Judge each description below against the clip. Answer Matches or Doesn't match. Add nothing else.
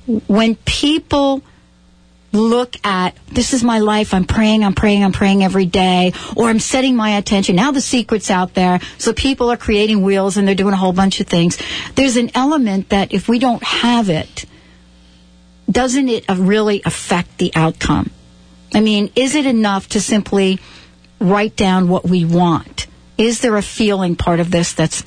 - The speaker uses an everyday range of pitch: Matches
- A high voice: Matches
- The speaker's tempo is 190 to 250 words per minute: Doesn't match